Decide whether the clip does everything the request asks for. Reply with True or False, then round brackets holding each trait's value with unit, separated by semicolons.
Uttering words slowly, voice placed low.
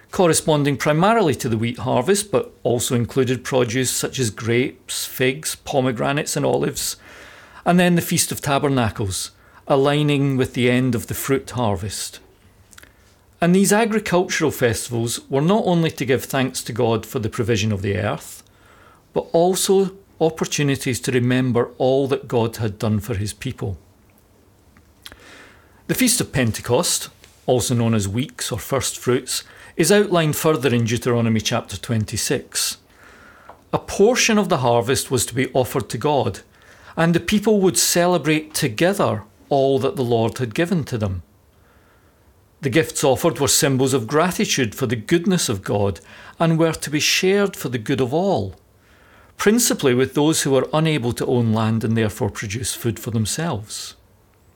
False (155 wpm; 130 Hz)